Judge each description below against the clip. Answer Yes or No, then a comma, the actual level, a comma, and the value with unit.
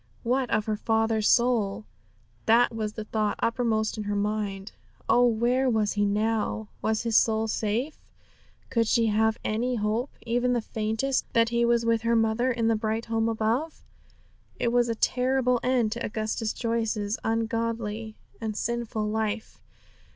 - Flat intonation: Yes, narrow, 1.6 semitones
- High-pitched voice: Yes, high, 225 Hz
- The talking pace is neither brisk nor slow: Yes, average, 160 wpm